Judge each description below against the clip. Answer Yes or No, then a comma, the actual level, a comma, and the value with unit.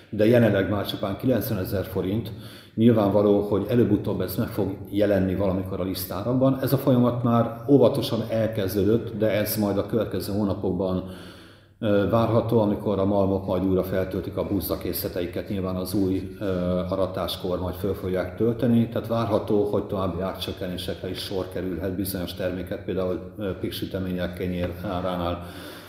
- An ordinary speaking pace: Yes, average, 140 wpm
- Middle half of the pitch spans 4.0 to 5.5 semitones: No, average, 2.7 semitones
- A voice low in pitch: Yes, low, 100 Hz